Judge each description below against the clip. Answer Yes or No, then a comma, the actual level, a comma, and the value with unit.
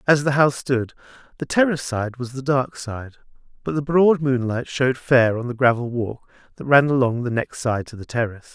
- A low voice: Yes, low, 130 Hz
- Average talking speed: No, fast, 210 wpm